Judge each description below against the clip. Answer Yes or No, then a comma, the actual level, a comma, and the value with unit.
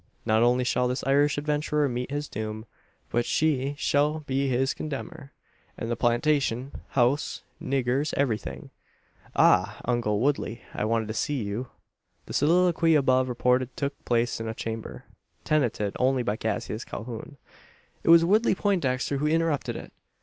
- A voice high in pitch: No, low, 130 Hz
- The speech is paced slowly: No, average, 150 wpm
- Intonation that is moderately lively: Yes, average, 3.8 semitones